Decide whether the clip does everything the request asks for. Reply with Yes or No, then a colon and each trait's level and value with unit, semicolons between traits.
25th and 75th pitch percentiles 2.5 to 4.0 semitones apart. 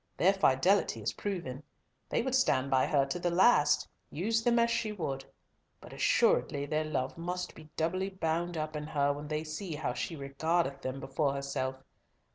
No: average, 4.7 semitones